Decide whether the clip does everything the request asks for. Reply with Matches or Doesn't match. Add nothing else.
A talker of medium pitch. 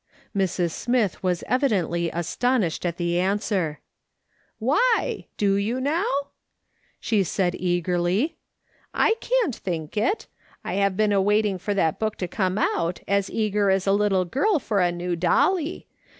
Doesn't match